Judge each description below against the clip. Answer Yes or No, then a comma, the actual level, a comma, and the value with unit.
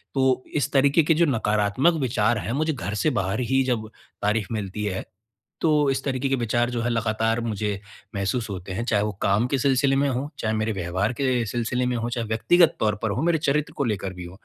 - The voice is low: Yes, low, 120 Hz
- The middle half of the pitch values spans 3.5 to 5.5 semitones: Yes, average, 4.1 semitones